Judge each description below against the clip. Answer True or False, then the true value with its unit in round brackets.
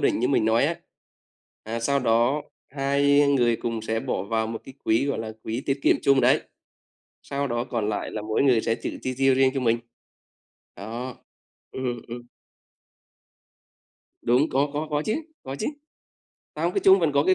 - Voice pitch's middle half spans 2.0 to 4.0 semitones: True (3.7 semitones)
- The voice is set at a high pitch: False (130 Hz)